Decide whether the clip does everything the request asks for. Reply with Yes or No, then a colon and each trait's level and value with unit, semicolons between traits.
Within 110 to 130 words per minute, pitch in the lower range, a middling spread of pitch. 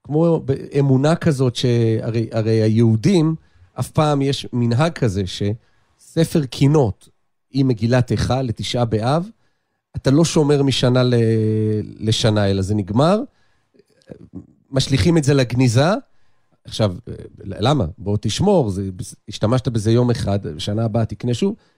Yes: average, 120 wpm; low, 120 Hz; average, 4.5 semitones